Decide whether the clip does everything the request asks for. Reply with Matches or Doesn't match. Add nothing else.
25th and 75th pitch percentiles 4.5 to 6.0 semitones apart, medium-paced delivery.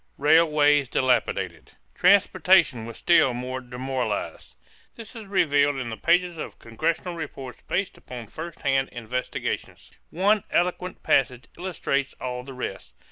Doesn't match